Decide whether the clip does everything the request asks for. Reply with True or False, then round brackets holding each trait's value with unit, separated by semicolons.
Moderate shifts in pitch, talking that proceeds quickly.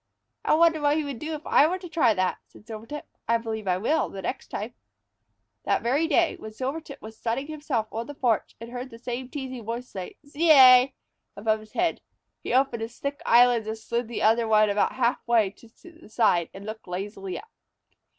True (4.7 semitones; 210 wpm)